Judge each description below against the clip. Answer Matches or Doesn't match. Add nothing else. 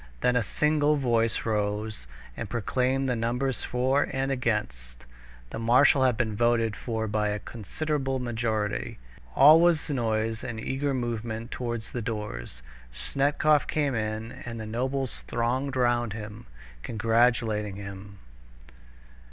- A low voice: Matches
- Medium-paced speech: Doesn't match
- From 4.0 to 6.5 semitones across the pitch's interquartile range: Doesn't match